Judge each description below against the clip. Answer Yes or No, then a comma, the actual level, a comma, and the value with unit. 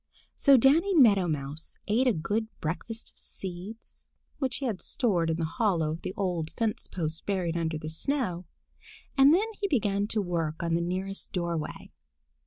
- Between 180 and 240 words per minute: No, average, 170 wpm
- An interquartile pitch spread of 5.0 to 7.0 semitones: Yes, wide, 5.6 semitones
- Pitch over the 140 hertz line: Yes, high, 190 Hz